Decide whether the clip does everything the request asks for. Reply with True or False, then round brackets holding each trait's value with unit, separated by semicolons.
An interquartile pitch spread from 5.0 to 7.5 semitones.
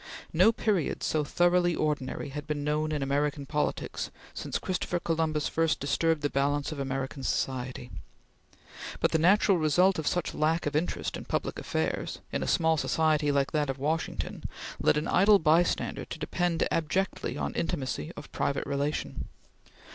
False (2.6 semitones)